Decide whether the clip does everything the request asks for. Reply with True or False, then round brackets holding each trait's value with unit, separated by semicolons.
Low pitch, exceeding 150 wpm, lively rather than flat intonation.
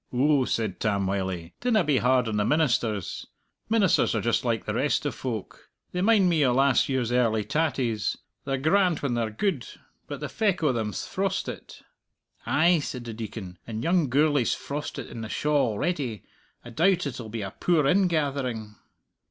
True (130 Hz; 175 wpm; 5.8 semitones)